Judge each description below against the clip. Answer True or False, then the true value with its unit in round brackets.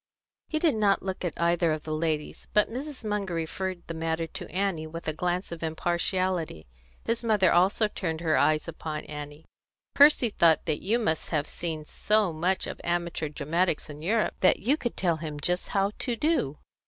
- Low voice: False (175 Hz)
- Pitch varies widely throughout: False (4.1 semitones)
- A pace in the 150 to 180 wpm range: False (190 wpm)